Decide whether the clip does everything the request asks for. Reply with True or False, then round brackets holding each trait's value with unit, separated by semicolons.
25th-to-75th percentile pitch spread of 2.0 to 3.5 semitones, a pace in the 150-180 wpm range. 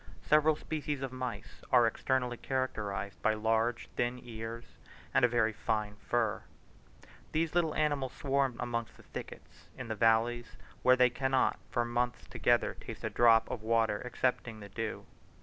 True (2.5 semitones; 155 wpm)